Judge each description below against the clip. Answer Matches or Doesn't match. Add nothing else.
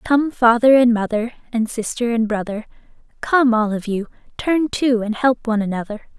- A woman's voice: Matches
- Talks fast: Doesn't match